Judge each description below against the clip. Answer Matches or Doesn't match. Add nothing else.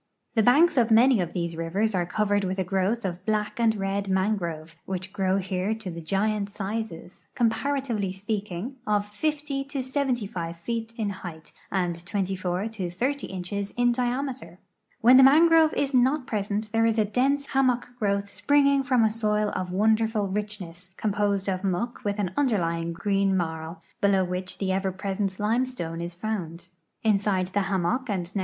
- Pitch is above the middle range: Matches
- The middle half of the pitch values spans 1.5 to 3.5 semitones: Doesn't match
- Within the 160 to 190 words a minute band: Matches